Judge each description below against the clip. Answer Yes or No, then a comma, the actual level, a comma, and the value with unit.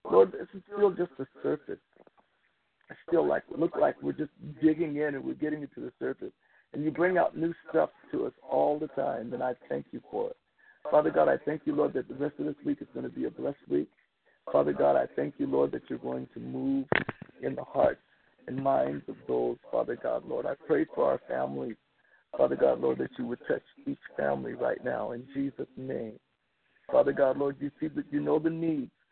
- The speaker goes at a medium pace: No, fast, 225 wpm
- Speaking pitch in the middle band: Yes, medium, 145 Hz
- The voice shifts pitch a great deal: Yes, wide, 5.8 semitones